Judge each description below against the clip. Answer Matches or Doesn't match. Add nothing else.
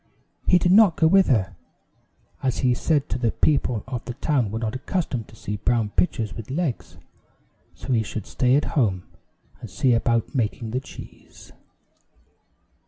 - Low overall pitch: Matches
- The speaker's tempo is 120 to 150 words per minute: Doesn't match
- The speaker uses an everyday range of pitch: Matches